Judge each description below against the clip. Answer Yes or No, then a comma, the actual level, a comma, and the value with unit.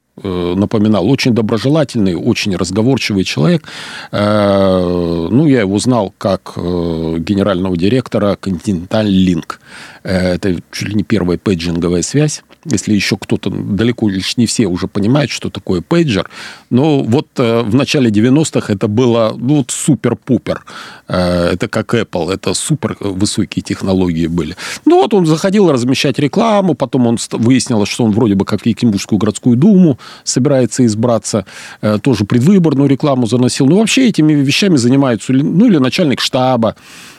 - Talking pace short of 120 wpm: No, average, 135 wpm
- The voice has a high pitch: No, low, 115 Hz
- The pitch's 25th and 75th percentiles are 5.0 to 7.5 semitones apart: Yes, wide, 5.6 semitones